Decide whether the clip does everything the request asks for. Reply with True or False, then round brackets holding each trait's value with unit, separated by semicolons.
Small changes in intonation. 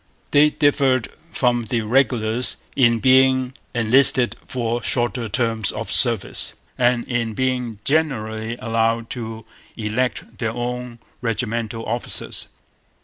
True (2.1 semitones)